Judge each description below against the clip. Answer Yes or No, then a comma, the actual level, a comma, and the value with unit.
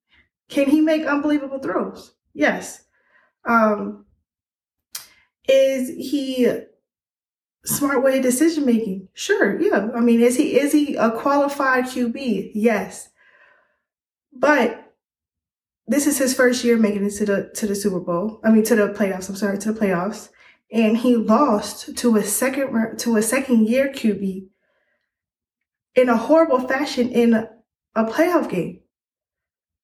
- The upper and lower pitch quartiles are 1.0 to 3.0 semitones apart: No, average, 4.2 semitones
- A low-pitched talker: No, high, 235 Hz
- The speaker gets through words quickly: No, slow, 135 wpm